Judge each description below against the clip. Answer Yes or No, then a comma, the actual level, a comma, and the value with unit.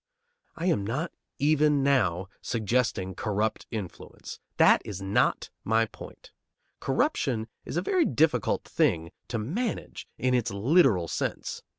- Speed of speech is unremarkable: No, slow, 125 wpm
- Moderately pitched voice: No, low, 115 Hz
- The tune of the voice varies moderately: No, wide, 6.8 semitones